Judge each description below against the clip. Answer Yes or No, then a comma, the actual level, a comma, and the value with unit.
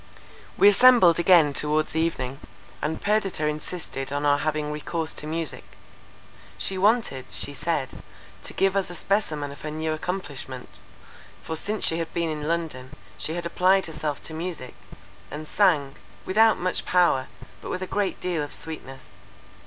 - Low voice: No, medium, 160 Hz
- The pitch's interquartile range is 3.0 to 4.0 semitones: Yes, average, 3.7 semitones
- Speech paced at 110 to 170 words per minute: Yes, average, 160 wpm